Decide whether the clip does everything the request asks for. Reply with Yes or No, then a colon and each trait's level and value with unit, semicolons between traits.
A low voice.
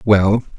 Yes: low, 105 Hz